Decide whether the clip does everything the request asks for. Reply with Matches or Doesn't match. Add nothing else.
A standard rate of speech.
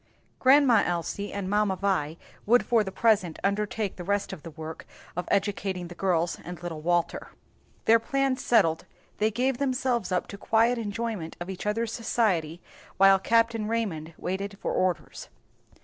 Matches